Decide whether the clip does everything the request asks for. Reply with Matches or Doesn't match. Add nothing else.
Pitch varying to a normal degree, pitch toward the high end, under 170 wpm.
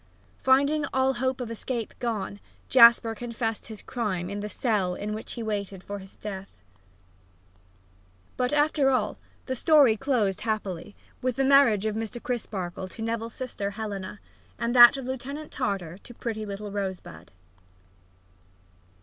Matches